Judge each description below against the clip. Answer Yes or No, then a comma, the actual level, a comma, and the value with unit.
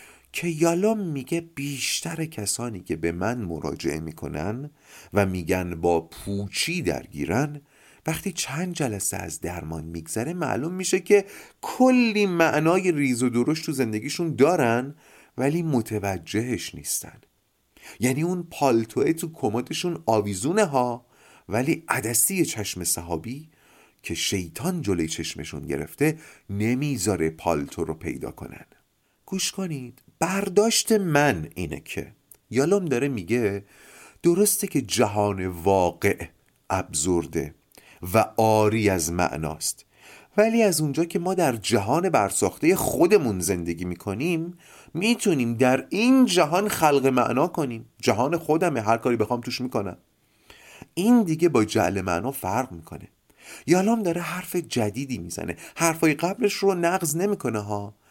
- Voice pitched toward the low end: Yes, low, 130 Hz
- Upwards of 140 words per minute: No, average, 120 wpm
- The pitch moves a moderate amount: No, wide, 8.9 semitones